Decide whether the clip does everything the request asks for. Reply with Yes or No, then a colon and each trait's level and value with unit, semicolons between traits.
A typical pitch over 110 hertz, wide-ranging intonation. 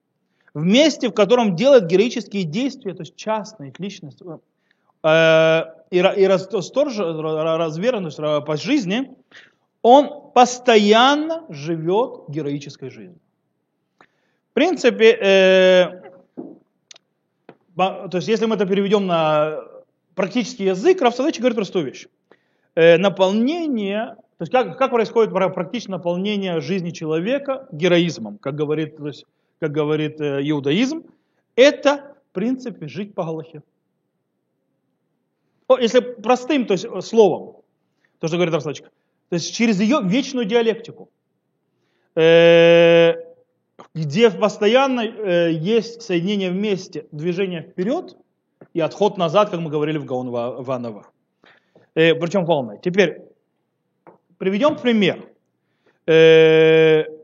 Yes: high, 190 Hz; wide, 6.5 semitones